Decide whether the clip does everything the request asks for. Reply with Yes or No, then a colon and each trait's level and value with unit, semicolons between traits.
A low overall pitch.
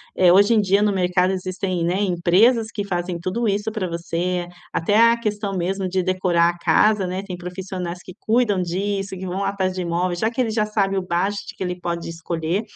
No: medium, 185 Hz